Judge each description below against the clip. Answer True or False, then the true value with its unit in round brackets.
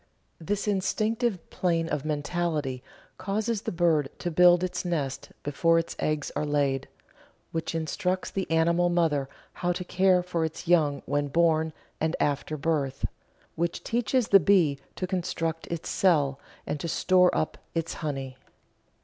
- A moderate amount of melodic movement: True (3.4 semitones)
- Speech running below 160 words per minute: True (150 wpm)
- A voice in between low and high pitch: True (165 Hz)